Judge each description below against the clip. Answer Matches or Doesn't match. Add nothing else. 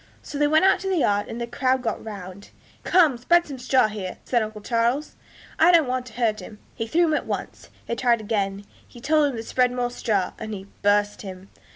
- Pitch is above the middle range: Matches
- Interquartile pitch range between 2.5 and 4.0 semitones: Doesn't match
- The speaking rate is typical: Doesn't match